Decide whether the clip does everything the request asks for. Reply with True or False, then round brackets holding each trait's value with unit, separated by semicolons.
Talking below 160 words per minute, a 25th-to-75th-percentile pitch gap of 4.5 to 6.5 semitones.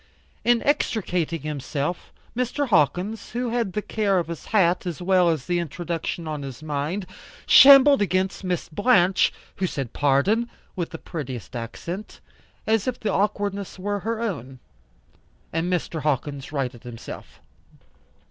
True (140 wpm; 5.6 semitones)